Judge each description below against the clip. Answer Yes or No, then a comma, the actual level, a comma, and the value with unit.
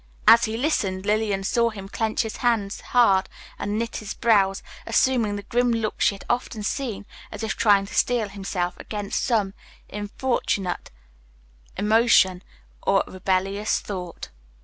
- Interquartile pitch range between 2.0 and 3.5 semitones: Yes, average, 2.9 semitones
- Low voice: No, high, 210 Hz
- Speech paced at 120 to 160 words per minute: Yes, average, 145 wpm